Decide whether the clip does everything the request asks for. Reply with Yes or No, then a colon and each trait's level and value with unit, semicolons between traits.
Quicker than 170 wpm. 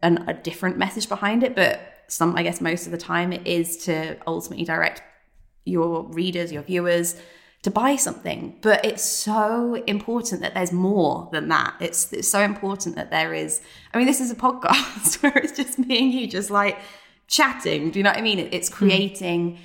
Yes: average, 200 wpm